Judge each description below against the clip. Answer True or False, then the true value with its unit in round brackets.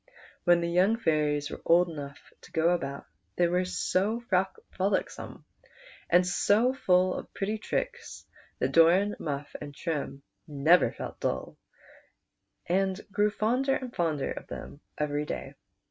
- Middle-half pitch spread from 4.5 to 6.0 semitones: True (5.0 semitones)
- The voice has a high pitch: False (175 Hz)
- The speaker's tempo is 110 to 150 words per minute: True (140 wpm)